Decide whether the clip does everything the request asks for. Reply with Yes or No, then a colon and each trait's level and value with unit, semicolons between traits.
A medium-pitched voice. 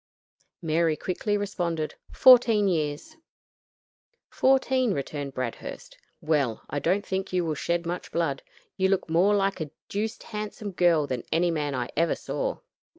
Yes: medium, 175 Hz